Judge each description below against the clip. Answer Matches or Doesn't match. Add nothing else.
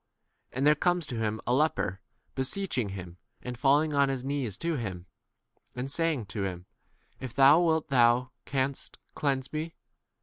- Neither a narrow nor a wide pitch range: Matches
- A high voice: Doesn't match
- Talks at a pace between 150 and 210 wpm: Matches